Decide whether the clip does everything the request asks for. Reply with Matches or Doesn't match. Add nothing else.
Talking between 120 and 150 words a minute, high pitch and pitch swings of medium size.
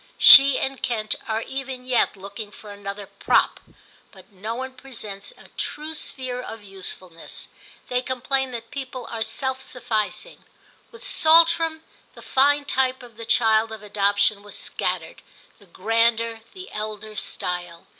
Matches